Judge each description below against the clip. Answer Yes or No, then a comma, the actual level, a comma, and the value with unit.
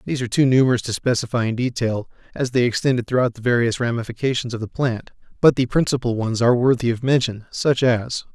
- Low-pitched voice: Yes, low, 120 Hz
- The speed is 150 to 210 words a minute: Yes, average, 200 wpm